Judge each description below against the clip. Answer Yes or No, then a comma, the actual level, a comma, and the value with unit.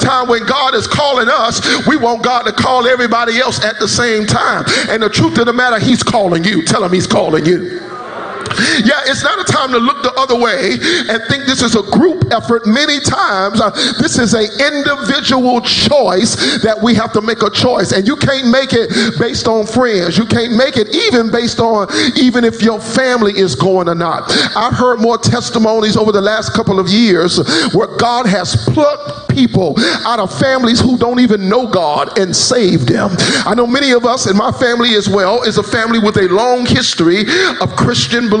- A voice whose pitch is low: No, high, 230 Hz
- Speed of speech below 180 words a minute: No, fast, 205 wpm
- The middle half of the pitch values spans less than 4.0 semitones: Yes, average, 3.0 semitones